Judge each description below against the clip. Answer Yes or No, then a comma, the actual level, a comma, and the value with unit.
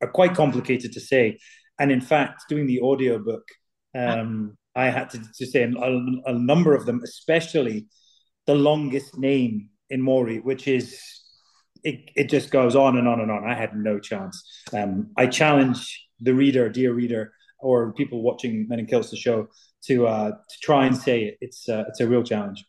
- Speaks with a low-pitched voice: Yes, low, 125 Hz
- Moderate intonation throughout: Yes, average, 3.3 semitones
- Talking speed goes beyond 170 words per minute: Yes, average, 185 wpm